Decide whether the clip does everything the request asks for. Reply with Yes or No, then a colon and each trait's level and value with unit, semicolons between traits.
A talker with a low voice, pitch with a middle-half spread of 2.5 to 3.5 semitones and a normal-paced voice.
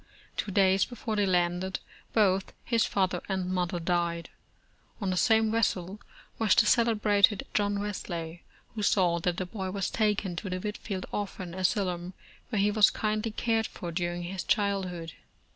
No: high, 190 Hz; average, 2.9 semitones; average, 165 wpm